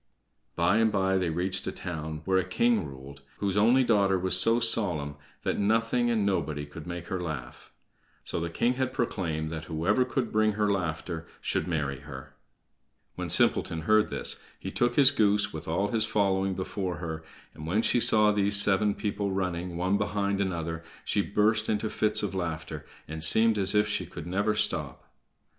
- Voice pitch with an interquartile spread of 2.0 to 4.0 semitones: No, average, 4.4 semitones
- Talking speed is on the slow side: No, average, 185 wpm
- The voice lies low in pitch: Yes, very low, 95 Hz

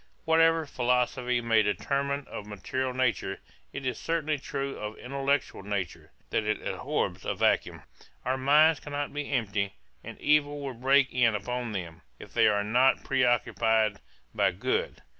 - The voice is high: No, low, 125 Hz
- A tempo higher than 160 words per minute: No, average, 155 wpm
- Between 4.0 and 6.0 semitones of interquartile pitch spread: Yes, average, 4.3 semitones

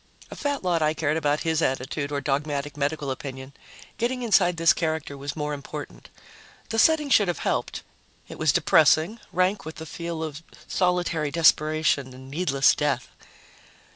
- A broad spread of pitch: No, average, 3.6 semitones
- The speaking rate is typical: Yes, average, 160 wpm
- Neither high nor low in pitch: Yes, medium, 155 Hz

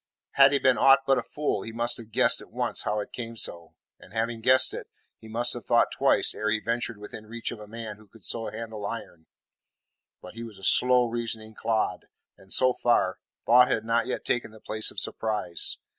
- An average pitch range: No, narrow, 1.8 semitones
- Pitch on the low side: Yes, low, 115 Hz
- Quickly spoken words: Yes, fast, 220 wpm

